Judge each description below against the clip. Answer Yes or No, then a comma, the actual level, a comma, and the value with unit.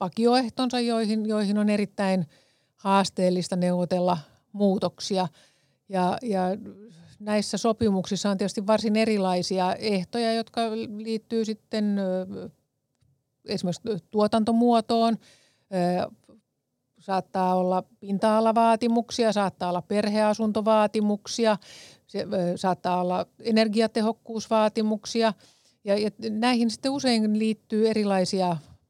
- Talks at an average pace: No, slow, 75 wpm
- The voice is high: Yes, high, 210 Hz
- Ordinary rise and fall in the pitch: Yes, average, 3.3 semitones